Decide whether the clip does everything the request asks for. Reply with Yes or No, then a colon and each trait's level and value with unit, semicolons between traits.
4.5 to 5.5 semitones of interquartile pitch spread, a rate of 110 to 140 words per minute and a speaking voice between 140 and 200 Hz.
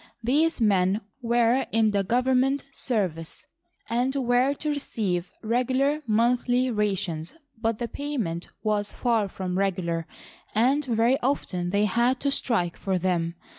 No: average, 5.0 semitones; slow, 135 wpm; high, 230 Hz